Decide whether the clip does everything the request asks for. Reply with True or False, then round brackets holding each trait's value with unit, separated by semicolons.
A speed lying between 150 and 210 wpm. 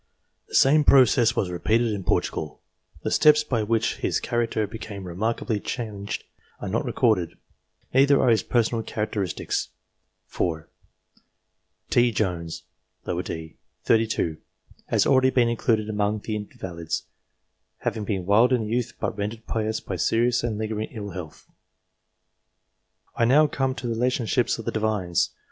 False (140 wpm)